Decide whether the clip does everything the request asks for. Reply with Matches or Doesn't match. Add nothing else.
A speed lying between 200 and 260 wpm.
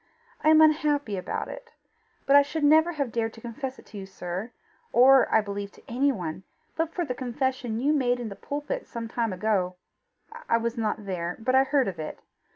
Matches